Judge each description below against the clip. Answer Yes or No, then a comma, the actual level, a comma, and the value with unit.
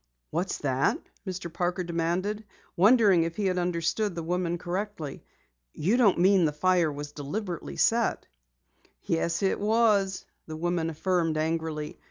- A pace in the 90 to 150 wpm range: Yes, average, 140 wpm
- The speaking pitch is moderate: Yes, medium, 175 Hz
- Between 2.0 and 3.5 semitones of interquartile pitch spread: Yes, average, 3.1 semitones